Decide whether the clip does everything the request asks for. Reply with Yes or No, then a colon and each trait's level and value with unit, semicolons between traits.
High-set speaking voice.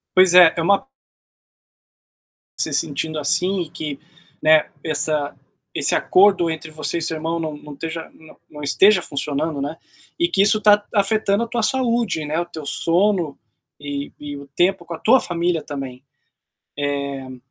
No: medium, 165 Hz